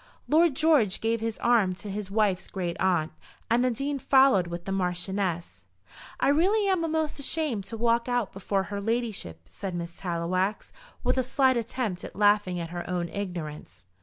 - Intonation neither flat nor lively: No, wide, 5.8 semitones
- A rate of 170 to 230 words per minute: Yes, average, 175 wpm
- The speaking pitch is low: No, high, 205 Hz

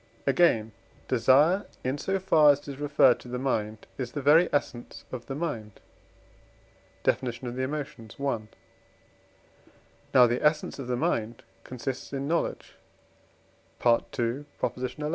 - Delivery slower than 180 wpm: Yes, average, 140 wpm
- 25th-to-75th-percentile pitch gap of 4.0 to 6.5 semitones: No, average, 3.4 semitones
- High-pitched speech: No, low, 130 Hz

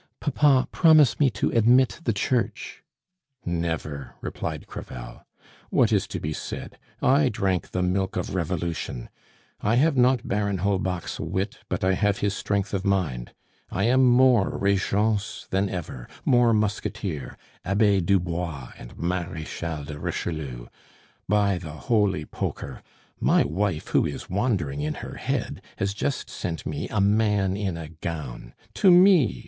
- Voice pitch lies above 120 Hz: No, low, 100 Hz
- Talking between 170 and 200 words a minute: No, average, 145 wpm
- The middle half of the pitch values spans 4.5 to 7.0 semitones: Yes, average, 5.1 semitones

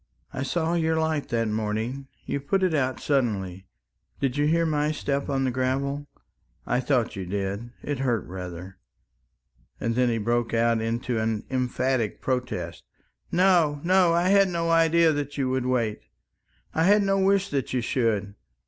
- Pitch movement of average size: No, wide, 5.7 semitones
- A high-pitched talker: No, low, 130 Hz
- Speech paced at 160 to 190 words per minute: Yes, average, 165 wpm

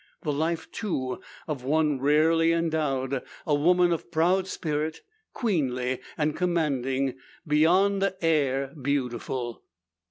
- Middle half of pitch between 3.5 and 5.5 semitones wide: Yes, average, 3.8 semitones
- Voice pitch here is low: No, medium, 150 Hz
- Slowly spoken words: Yes, slow, 105 wpm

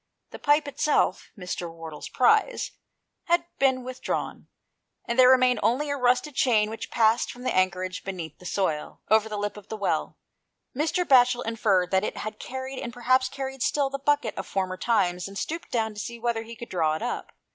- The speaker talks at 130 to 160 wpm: No, average, 200 wpm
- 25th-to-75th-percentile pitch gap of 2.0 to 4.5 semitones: No, average, 5.0 semitones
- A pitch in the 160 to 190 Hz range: No, high, 235 Hz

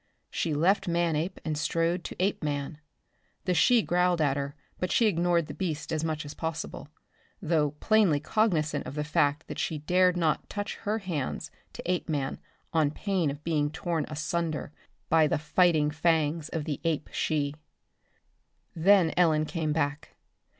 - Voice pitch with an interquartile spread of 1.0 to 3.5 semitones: Yes, average, 2.9 semitones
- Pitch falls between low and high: Yes, medium, 160 Hz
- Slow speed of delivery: No, average, 155 wpm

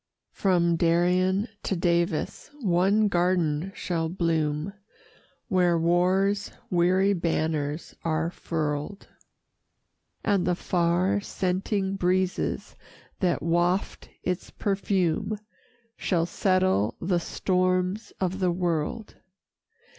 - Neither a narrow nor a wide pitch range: No, narrow, 2.1 semitones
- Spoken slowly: Yes, slow, 90 wpm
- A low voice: No, medium, 180 Hz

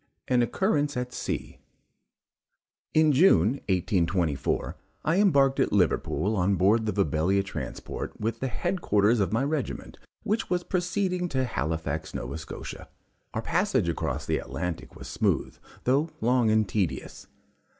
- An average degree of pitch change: No, wide, 7.9 semitones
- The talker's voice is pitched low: Yes, low, 115 Hz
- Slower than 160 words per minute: Yes, average, 140 wpm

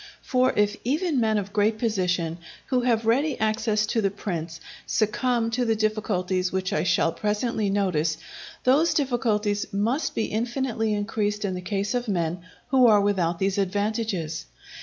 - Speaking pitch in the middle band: No, high, 210 Hz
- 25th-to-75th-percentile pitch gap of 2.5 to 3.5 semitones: Yes, average, 3.2 semitones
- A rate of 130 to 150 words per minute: No, average, 160 wpm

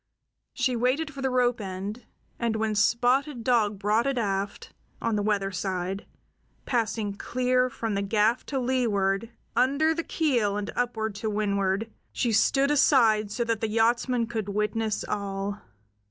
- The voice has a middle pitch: No, high, 225 Hz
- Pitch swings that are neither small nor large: Yes, average, 3.4 semitones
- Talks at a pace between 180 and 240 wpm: No, average, 155 wpm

